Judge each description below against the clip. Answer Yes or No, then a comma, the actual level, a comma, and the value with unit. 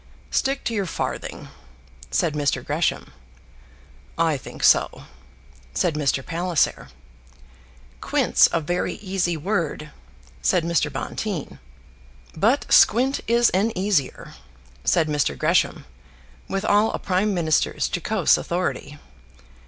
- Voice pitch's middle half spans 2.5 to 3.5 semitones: No, average, 5.2 semitones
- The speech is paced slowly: Yes, slow, 110 wpm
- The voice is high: No, medium, 175 Hz